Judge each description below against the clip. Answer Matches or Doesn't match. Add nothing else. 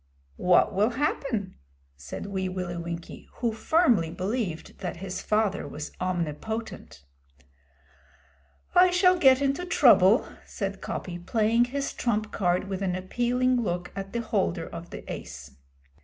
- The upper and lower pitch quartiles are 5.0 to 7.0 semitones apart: Matches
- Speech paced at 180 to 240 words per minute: Doesn't match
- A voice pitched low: Doesn't match